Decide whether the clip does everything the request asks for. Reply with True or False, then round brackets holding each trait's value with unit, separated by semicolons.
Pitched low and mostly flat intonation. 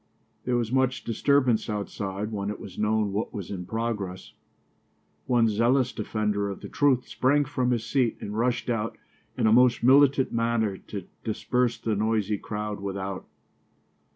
False (110 Hz; 3.2 semitones)